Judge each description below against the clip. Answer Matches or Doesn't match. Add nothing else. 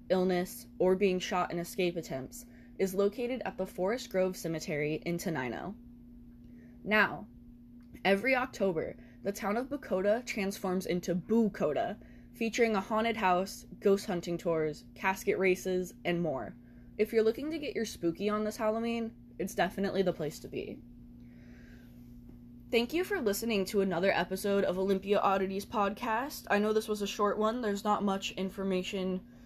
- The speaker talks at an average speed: Matches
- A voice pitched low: Doesn't match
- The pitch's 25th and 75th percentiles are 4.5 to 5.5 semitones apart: Matches